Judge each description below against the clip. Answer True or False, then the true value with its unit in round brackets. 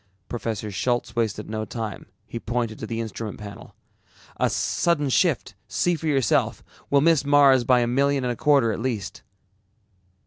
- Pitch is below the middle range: True (120 Hz)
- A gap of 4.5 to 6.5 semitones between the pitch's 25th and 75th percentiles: False (4.1 semitones)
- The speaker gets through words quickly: False (165 wpm)